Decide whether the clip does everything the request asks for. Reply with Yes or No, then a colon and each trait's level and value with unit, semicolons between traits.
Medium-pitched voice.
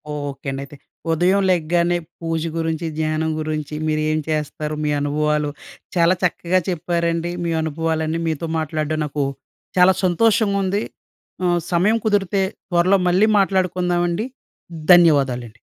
Yes: medium, 165 Hz